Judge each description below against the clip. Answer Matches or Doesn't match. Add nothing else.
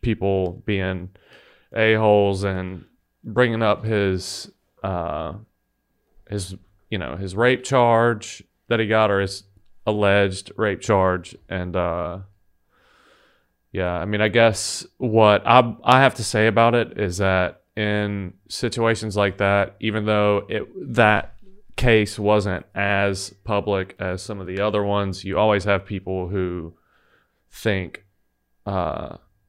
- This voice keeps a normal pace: Doesn't match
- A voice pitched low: Matches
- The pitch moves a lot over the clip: Doesn't match